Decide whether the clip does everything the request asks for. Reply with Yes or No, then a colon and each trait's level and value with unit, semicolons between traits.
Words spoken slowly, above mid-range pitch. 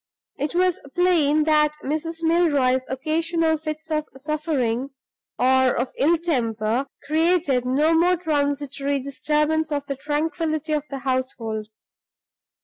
Yes: slow, 120 wpm; very high, 300 Hz